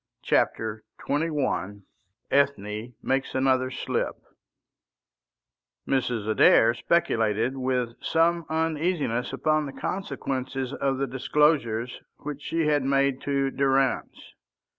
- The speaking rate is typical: No, slow, 95 wpm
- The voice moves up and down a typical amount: Yes, average, 3.4 semitones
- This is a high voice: No, low, 135 Hz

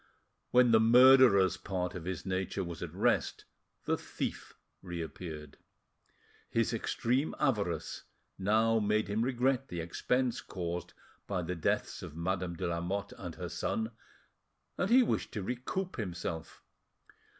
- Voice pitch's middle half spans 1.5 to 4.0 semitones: No, wide, 5.5 semitones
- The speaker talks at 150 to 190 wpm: No, slow, 135 wpm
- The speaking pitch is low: Yes, low, 100 Hz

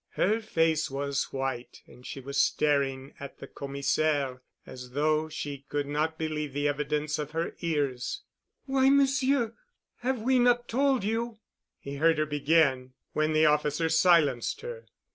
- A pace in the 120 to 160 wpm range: Yes, average, 150 wpm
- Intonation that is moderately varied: No, wide, 6.1 semitones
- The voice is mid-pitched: Yes, medium, 155 Hz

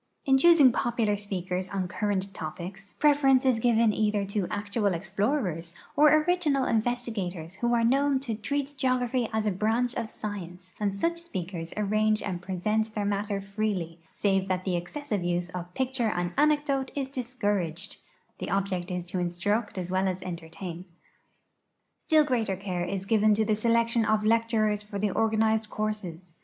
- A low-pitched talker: No, high, 210 Hz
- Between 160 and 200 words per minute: Yes, average, 165 wpm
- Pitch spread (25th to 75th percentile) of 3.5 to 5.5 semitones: Yes, average, 4.3 semitones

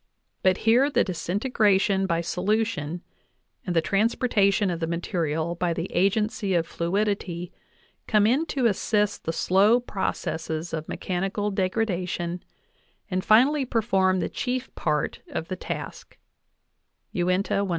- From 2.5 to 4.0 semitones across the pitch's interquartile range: Yes, average, 3.7 semitones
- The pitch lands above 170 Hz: Yes, high, 190 Hz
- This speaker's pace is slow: Yes, slow, 130 wpm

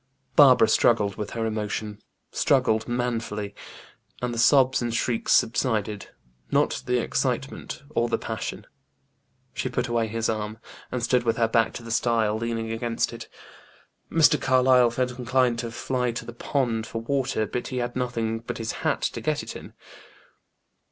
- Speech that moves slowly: No, average, 165 wpm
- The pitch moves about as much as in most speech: No, narrow, 1.8 semitones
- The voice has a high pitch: No, low, 115 Hz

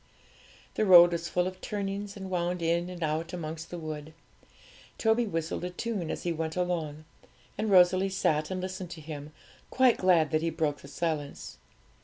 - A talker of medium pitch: Yes, medium, 170 Hz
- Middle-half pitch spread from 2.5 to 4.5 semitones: Yes, average, 2.9 semitones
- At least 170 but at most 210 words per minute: Yes, average, 180 wpm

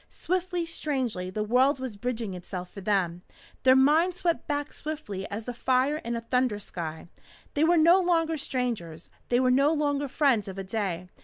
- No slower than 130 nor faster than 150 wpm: No, average, 180 wpm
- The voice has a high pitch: Yes, very high, 255 Hz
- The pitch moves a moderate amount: No, wide, 6.9 semitones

